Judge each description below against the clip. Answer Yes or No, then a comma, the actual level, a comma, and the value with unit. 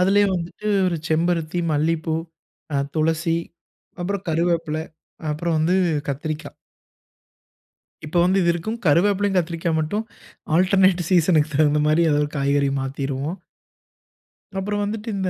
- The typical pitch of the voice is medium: Yes, medium, 165 Hz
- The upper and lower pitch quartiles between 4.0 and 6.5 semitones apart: No, average, 3.2 semitones